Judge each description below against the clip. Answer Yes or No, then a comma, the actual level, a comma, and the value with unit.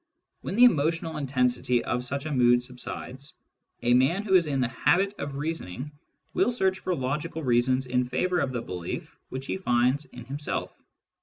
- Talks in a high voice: No, low, 135 Hz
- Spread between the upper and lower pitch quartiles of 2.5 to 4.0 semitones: No, average, 4.7 semitones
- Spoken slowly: No, average, 180 wpm